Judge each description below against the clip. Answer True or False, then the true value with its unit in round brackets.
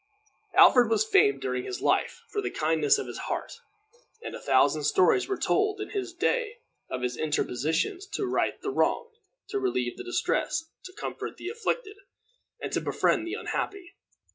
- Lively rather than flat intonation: True (8.9 semitones)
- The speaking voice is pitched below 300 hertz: False (385 Hz)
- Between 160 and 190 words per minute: True (175 wpm)